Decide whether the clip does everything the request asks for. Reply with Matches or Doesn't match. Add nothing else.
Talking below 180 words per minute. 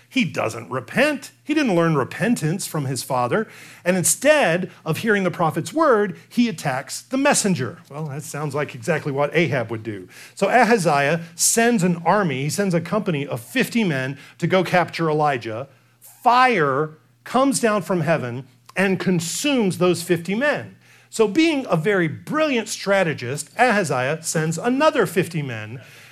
Matches